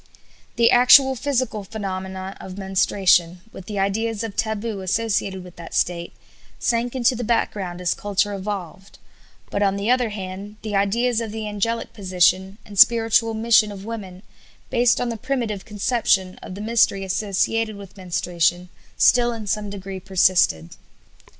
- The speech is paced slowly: No, average, 150 wpm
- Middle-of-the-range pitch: No, high, 205 Hz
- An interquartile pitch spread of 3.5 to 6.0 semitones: No, average, 3.1 semitones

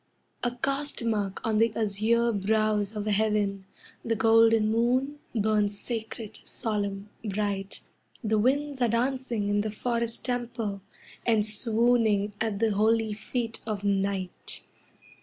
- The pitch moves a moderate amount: No, narrow, 2.2 semitones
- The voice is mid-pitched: No, high, 220 Hz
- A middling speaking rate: No, slow, 125 wpm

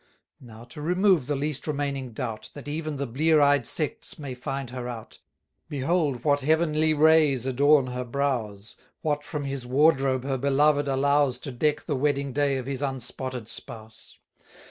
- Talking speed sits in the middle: Yes, average, 165 wpm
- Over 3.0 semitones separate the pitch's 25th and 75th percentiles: No, average, 2.7 semitones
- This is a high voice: No, medium, 140 Hz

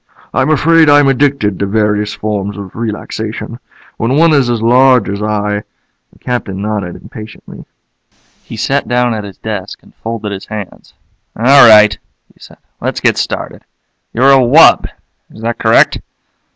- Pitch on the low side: Yes, low, 110 Hz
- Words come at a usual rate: Yes, average, 160 wpm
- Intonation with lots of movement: No, average, 3.7 semitones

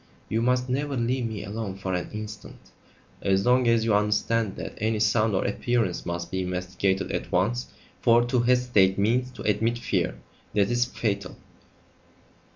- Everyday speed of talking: Yes, average, 160 wpm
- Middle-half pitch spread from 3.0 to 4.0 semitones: Yes, average, 3.7 semitones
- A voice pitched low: Yes, low, 110 Hz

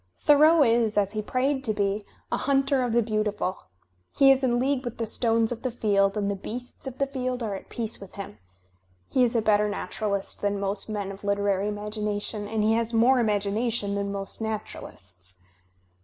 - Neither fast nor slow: Yes, average, 195 wpm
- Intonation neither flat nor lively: Yes, average, 3.3 semitones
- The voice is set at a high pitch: Yes, high, 215 Hz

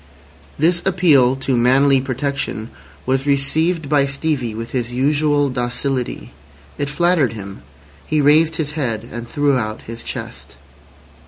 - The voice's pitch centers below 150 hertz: Yes, medium, 140 Hz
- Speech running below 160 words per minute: Yes, slow, 135 wpm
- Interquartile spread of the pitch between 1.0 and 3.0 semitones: No, average, 3.4 semitones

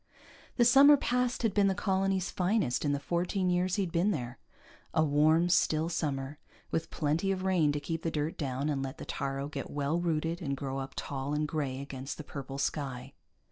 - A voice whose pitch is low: No, medium, 155 Hz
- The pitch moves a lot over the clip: No, average, 4.7 semitones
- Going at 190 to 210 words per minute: Yes, average, 200 wpm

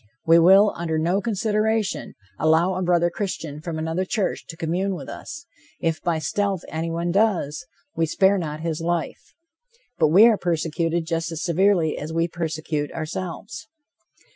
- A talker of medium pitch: Yes, medium, 170 Hz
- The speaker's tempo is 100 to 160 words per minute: Yes, average, 155 wpm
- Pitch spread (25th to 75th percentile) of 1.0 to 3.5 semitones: Yes, average, 2.9 semitones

